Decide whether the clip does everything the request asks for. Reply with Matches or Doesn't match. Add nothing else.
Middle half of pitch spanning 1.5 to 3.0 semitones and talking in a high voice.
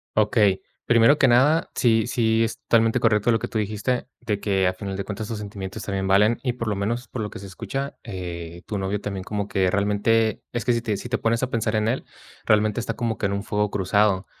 Doesn't match